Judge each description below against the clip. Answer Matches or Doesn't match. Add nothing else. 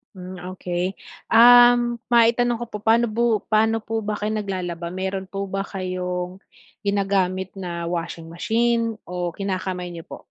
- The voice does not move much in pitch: Doesn't match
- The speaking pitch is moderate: Doesn't match